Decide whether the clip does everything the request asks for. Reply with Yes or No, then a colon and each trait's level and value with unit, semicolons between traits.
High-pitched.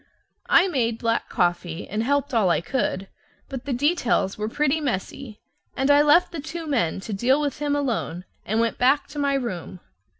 Yes: very high, 250 Hz